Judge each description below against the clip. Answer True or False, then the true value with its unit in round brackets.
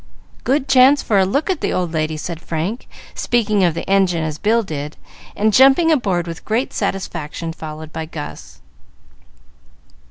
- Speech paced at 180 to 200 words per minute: False (160 wpm)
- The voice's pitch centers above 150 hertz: True (185 Hz)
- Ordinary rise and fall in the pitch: False (6.6 semitones)